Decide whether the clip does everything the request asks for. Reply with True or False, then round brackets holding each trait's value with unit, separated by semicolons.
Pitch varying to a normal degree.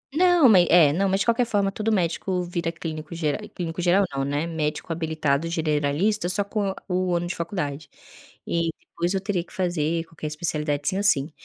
True (3.7 semitones)